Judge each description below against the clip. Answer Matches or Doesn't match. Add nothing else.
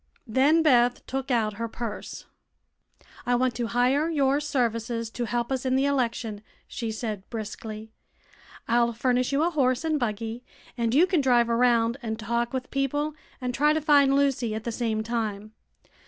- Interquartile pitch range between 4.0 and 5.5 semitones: Doesn't match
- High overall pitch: Matches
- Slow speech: Doesn't match